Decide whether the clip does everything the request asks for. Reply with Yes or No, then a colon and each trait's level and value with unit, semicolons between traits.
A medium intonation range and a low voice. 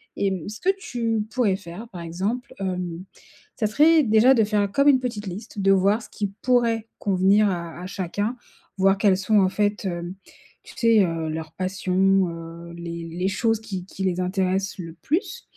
No: average, 3.3 semitones; high, 195 Hz